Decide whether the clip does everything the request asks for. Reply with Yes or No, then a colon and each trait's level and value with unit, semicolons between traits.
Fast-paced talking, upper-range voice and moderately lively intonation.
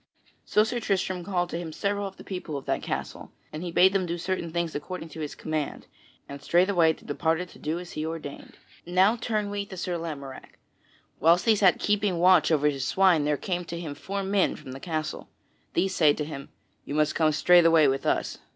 No: fast, 215 wpm; medium, 170 Hz; average, 3.4 semitones